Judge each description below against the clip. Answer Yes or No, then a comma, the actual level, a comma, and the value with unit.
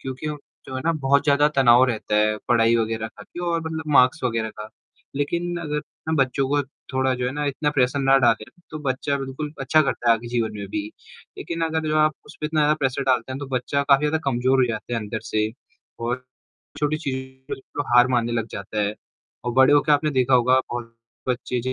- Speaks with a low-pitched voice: Yes, low, 130 Hz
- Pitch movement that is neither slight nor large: Yes, average, 3.6 semitones